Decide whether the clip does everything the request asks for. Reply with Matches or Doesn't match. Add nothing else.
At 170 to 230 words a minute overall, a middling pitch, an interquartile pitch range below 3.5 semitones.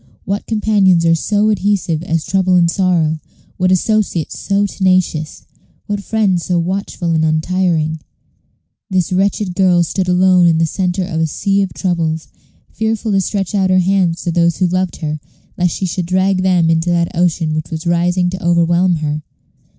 Matches